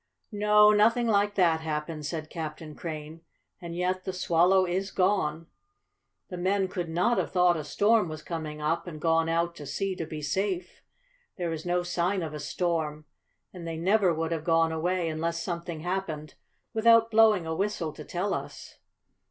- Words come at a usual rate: Yes, average, 175 wpm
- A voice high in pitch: No, medium, 170 Hz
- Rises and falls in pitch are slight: No, average, 3.0 semitones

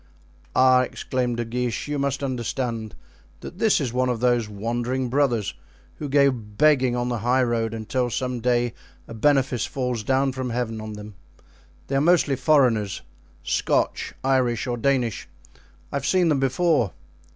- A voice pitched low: Yes, low, 125 Hz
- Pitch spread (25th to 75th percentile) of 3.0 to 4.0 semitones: No, narrow, 2.6 semitones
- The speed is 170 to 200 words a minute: No, average, 155 wpm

